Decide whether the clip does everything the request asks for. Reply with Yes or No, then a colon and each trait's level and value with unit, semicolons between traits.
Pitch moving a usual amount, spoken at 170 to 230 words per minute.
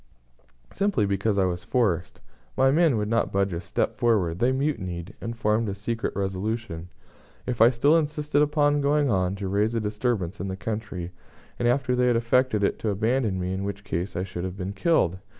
Yes: average, 4.7 semitones; average, 200 wpm